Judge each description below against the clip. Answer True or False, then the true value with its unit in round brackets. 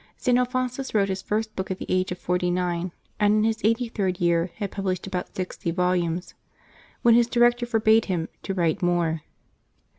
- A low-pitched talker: False (190 Hz)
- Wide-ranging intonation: False (3.9 semitones)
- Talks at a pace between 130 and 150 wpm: False (185 wpm)